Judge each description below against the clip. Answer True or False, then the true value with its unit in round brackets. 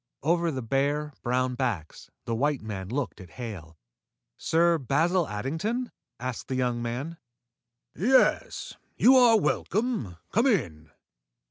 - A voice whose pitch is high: False (135 Hz)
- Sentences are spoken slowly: True (125 wpm)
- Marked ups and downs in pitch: True (6.7 semitones)